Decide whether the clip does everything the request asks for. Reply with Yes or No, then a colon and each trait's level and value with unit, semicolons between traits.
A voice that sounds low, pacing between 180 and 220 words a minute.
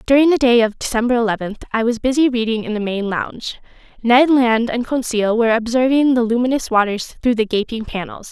No: high, 235 Hz; average, 195 wpm